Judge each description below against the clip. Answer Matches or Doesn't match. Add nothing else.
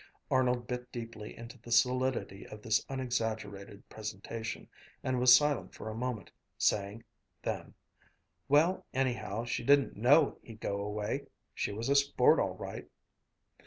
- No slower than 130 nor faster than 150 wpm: Matches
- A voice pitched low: Matches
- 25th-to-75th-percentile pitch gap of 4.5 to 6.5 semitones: Doesn't match